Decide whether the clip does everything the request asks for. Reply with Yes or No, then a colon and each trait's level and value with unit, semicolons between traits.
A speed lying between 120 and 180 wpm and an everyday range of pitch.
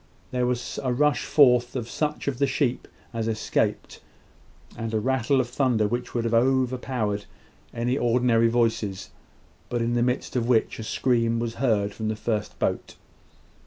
No: average, 165 wpm; narrow, 2.0 semitones